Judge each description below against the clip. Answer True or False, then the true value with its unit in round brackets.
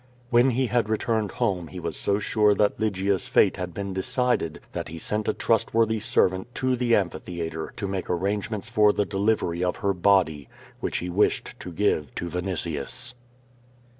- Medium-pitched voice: False (100 Hz)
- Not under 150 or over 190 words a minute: True (170 wpm)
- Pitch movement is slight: False (3.8 semitones)